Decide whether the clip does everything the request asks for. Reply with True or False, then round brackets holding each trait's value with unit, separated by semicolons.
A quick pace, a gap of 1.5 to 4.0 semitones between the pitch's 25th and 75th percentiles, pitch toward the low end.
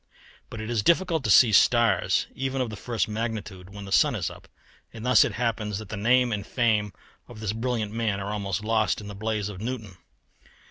True (215 wpm; 2.5 semitones; 110 Hz)